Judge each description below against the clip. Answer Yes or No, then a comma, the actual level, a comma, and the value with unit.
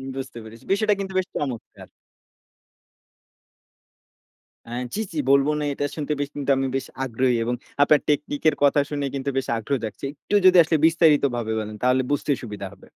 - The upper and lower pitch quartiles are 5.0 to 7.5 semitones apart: No, average, 3.7 semitones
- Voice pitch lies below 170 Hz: Yes, medium, 140 Hz